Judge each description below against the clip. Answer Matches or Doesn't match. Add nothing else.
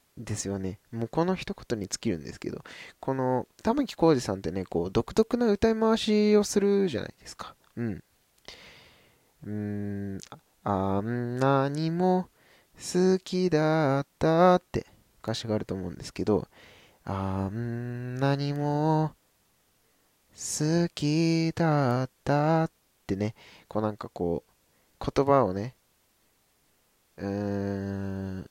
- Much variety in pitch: Matches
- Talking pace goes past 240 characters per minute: Doesn't match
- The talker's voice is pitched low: Matches